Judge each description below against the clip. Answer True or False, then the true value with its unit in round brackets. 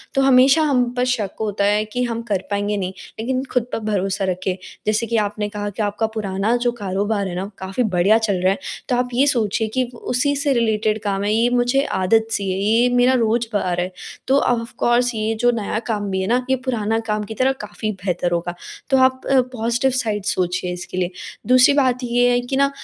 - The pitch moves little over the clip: False (3.5 semitones)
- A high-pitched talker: True (220 Hz)